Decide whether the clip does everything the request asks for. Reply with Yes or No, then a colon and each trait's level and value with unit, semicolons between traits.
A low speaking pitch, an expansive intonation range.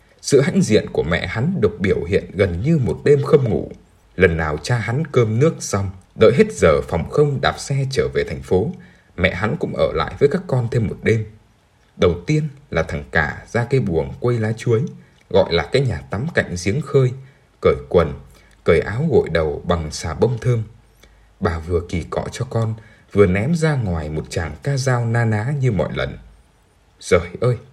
Yes: low, 115 Hz; wide, 5.8 semitones